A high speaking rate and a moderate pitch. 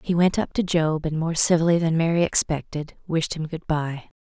Yes: fast, 215 wpm; medium, 165 Hz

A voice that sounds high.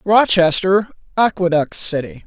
No: medium, 180 Hz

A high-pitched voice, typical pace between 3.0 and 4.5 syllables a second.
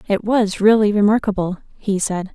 No: high, 205 Hz; 5.0 syllables/s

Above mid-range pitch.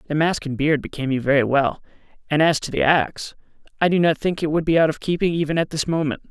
No: medium, 155 Hz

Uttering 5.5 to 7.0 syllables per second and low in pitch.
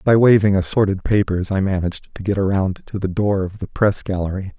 Yes: 5.7 syllables/s; very low, 95 Hz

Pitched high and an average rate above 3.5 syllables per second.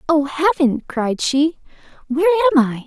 Yes: very high, 270 Hz; 4.9 syllables/s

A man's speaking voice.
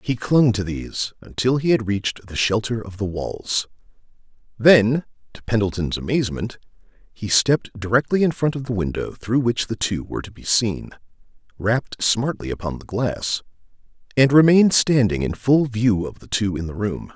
Yes: male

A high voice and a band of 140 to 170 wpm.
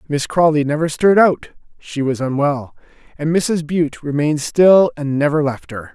No: medium, 150 Hz; average, 150 wpm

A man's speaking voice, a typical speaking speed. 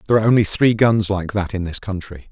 No: male; fast, 260 wpm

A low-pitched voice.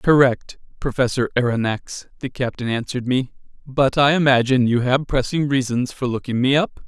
Yes: low, 130 Hz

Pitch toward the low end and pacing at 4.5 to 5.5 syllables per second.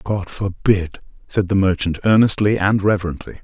Yes: very low, 95 Hz; 5.1 syllables/s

